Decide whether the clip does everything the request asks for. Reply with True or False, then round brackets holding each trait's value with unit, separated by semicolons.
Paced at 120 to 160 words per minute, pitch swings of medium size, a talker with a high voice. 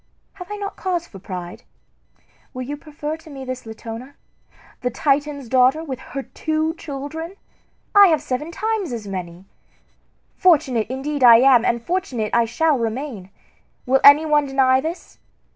True (155 wpm; 4.8 semitones; 275 Hz)